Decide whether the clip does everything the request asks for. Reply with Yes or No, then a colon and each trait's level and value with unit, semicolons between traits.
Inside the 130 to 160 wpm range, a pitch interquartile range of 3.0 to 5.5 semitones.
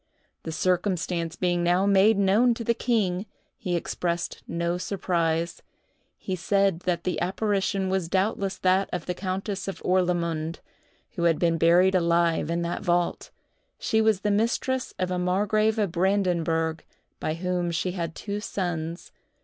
No: average, 150 wpm; narrow, 2.5 semitones